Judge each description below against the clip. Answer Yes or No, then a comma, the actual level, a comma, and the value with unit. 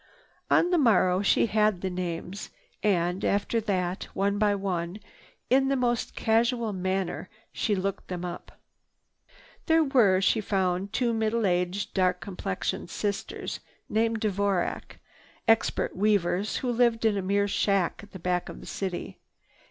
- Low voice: No, high, 200 Hz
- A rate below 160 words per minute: Yes, average, 145 wpm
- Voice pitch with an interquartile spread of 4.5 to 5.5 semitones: No, average, 3.2 semitones